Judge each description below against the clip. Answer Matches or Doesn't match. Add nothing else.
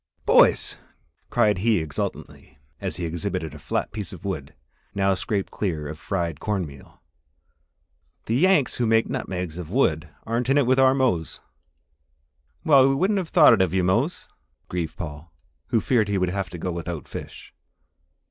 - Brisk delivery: Doesn't match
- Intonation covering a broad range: Matches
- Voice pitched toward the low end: Matches